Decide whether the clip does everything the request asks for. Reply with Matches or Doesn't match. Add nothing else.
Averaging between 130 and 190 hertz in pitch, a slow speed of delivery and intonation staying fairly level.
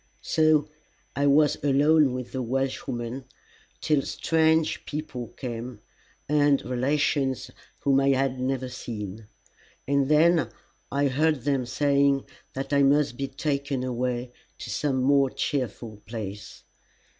Matches